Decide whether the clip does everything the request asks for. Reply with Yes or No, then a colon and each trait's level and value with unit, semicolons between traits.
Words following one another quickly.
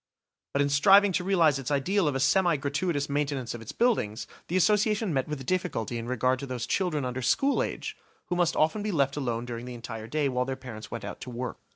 Yes: fast, 235 wpm